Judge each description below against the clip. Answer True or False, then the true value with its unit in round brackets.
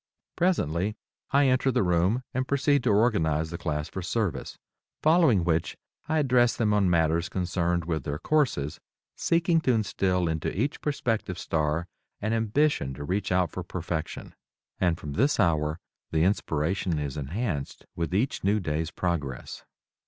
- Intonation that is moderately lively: False (7.0 semitones)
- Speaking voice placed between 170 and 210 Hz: False (90 Hz)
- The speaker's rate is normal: True (150 wpm)